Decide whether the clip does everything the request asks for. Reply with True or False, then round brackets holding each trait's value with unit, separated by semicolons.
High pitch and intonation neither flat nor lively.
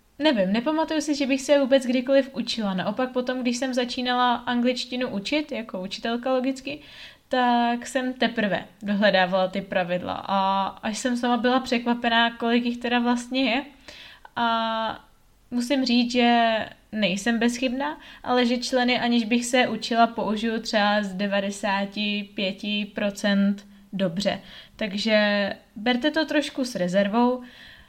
True (235 Hz; 3.6 semitones)